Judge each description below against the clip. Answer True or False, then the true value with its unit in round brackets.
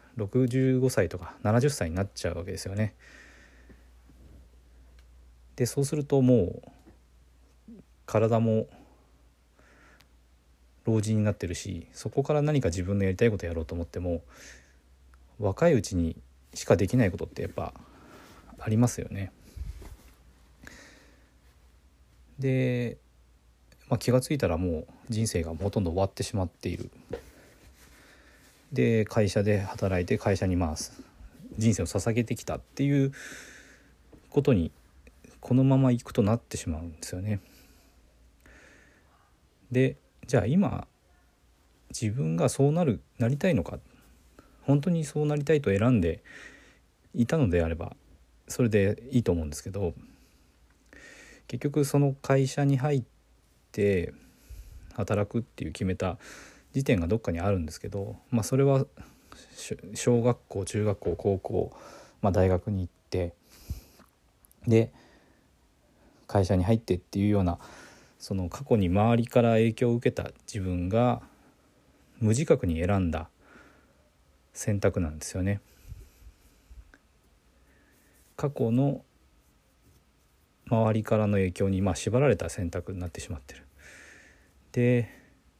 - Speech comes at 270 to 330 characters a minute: False (240 characters per minute)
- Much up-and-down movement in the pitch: True (7.8 semitones)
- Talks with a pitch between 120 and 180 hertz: False (95 Hz)